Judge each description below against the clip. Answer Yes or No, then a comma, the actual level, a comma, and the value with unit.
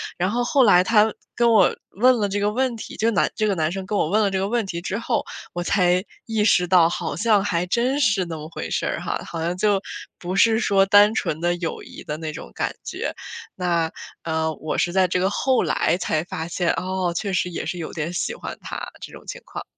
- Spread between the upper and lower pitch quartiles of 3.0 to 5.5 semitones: Yes, average, 3.8 semitones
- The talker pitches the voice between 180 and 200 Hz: Yes, high, 190 Hz